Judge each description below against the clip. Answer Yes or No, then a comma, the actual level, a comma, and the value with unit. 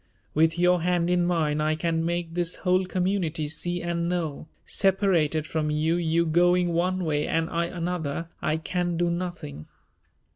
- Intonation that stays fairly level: Yes, narrow, 1.9 semitones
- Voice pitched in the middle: Yes, medium, 170 Hz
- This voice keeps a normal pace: Yes, average, 160 wpm